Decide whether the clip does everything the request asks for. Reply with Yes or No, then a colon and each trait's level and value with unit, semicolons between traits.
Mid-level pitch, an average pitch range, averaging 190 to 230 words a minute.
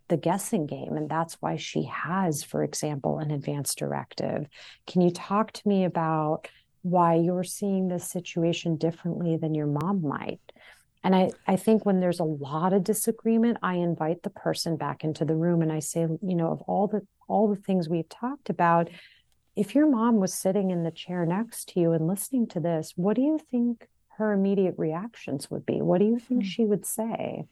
Yes: medium, 180 Hz; average, 3.9 semitones; average, 200 wpm